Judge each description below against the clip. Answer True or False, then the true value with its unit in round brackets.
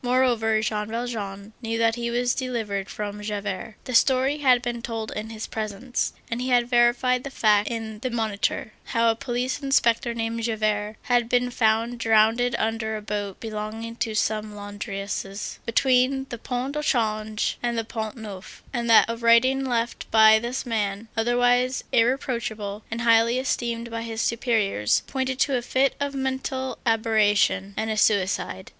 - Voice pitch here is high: True (230 Hz)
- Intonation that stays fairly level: True (2.3 semitones)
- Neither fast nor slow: True (165 wpm)